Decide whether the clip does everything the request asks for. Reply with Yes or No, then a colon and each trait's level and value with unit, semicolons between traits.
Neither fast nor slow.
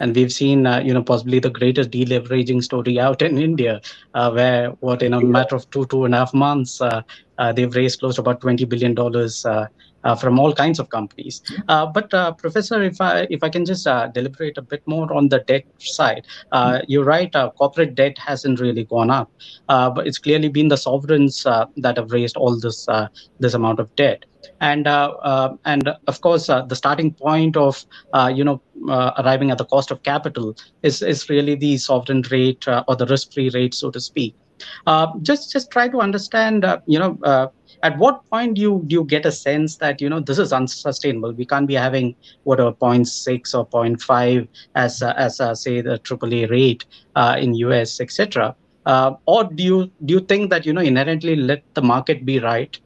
No: fast, 215 wpm